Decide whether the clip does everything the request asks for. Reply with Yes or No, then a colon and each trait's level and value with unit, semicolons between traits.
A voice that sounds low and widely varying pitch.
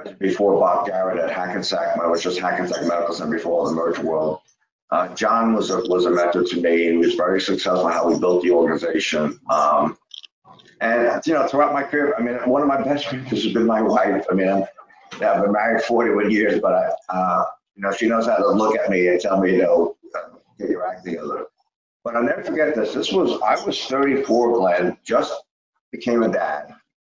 Yes: low, 100 Hz; wide, 5.7 semitones